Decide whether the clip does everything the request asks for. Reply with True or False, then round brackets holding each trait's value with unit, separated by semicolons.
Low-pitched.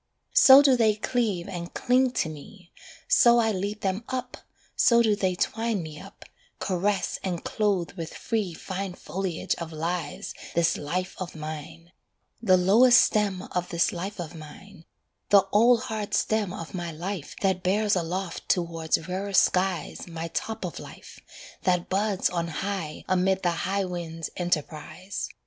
False (185 Hz)